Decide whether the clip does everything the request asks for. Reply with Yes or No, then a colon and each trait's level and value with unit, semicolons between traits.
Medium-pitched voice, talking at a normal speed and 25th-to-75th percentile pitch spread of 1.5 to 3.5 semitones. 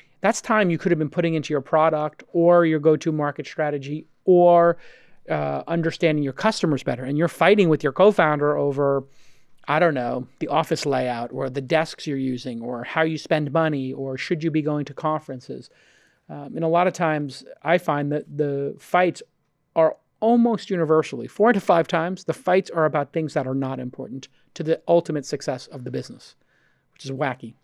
Yes: medium, 155 Hz; average, 195 wpm; average, 3.2 semitones